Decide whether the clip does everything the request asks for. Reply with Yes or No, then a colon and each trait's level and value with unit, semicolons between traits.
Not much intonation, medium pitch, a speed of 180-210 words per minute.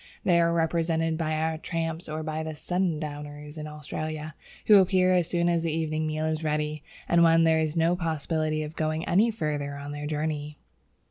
Yes: narrow, 1.6 semitones; medium, 160 Hz; average, 190 wpm